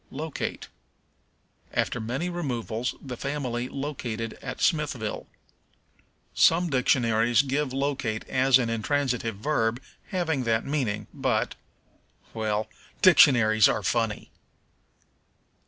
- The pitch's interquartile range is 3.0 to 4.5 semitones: Yes, average, 4.2 semitones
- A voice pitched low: Yes, low, 125 Hz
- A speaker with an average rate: No, slow, 95 wpm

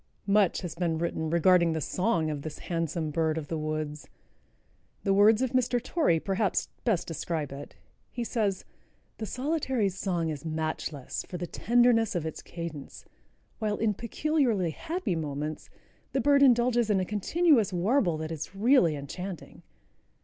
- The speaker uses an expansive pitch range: Yes, wide, 6.5 semitones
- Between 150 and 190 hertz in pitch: Yes, medium, 185 Hz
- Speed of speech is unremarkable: Yes, average, 155 wpm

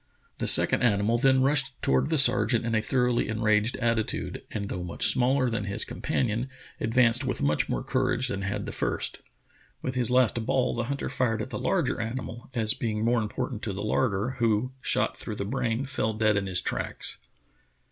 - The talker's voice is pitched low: Yes, low, 115 Hz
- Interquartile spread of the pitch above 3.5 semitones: No, average, 3.0 semitones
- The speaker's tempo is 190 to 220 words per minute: Yes, average, 200 wpm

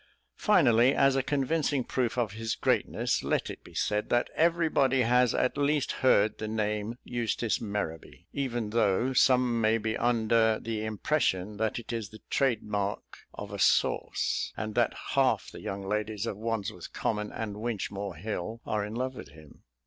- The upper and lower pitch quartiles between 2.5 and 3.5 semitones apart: Yes, average, 3.0 semitones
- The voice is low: Yes, low, 110 Hz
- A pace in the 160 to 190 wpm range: Yes, average, 170 wpm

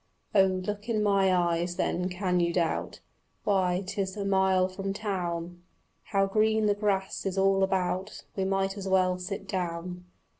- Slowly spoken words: No, average, 160 wpm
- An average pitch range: No, narrow, 1.5 semitones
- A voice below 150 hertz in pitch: No, high, 190 Hz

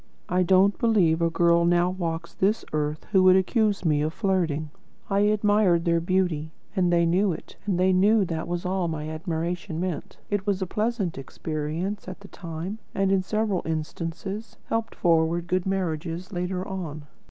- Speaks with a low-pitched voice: No, medium, 180 Hz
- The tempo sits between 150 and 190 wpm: Yes, average, 175 wpm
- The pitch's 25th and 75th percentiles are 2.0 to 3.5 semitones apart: Yes, average, 2.9 semitones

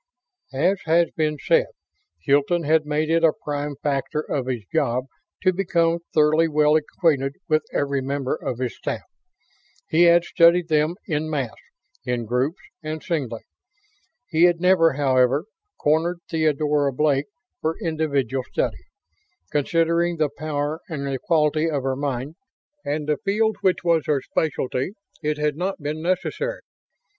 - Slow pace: No, average, 145 wpm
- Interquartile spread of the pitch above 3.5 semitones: No, average, 3.0 semitones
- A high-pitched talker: No, medium, 155 Hz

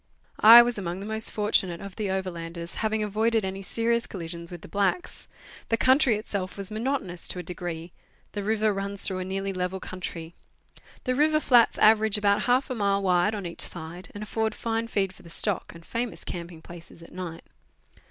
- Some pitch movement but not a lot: Yes, average, 3.6 semitones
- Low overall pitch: No, high, 200 Hz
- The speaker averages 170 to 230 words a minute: Yes, average, 190 wpm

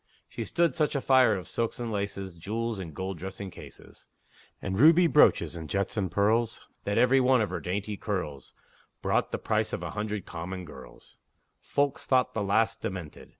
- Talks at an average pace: Yes, average, 185 wpm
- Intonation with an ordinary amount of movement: Yes, average, 4.2 semitones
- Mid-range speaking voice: No, low, 100 Hz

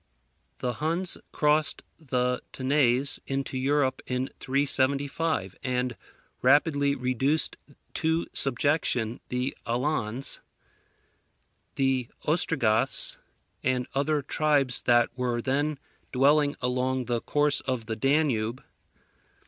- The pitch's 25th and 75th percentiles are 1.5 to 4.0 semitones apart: Yes, average, 2.7 semitones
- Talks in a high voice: No, low, 135 Hz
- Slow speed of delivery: Yes, slow, 95 wpm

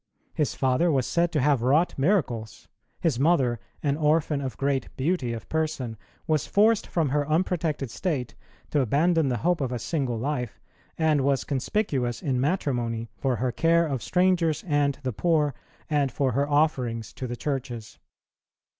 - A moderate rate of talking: Yes, average, 165 wpm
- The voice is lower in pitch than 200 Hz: Yes, medium, 140 Hz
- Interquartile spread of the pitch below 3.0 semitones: No, average, 4.0 semitones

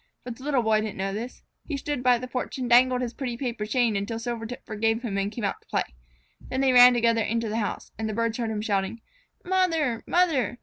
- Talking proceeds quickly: Yes, fast, 235 wpm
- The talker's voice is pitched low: No, high, 235 Hz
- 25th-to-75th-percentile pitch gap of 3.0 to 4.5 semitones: No, narrow, 2.4 semitones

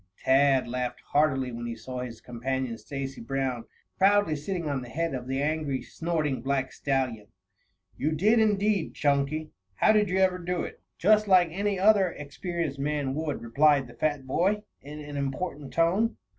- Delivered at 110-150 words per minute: No, average, 170 wpm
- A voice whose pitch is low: No, medium, 145 Hz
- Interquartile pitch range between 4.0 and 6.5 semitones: Yes, average, 5.2 semitones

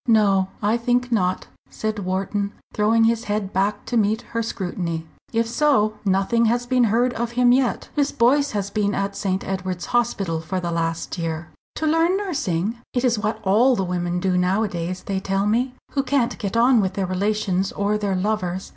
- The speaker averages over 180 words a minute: Yes, average, 190 wpm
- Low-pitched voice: No, high, 210 Hz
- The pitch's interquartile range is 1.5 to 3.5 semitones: No, average, 3.9 semitones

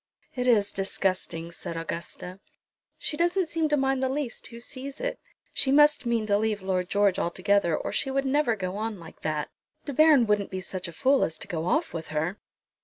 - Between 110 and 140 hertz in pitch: No, high, 215 Hz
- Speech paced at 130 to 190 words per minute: No, fast, 205 wpm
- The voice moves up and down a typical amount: No, wide, 6.9 semitones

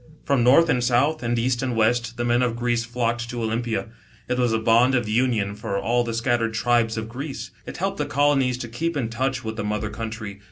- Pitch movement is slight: Yes, narrow, 1.8 semitones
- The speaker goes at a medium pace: No, fast, 230 wpm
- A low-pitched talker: Yes, low, 120 Hz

